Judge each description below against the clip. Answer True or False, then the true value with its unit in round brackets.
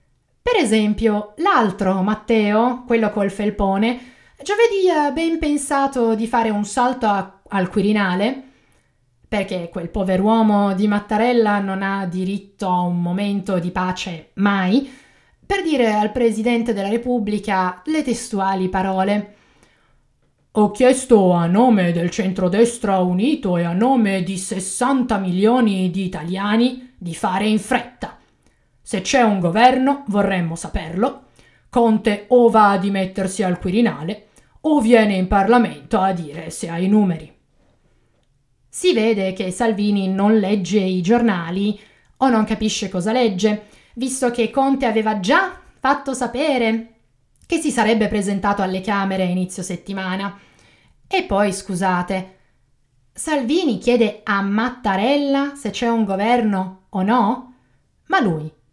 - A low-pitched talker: False (210 Hz)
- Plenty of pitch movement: False (4.1 semitones)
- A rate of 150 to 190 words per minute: False (130 wpm)